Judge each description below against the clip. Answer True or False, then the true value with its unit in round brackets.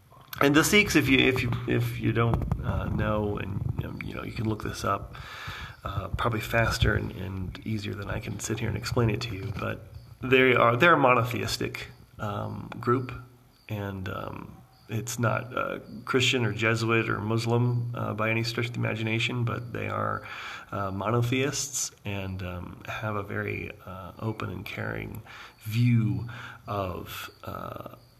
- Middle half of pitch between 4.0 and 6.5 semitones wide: False (2.6 semitones)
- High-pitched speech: False (110 Hz)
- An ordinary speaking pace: True (165 wpm)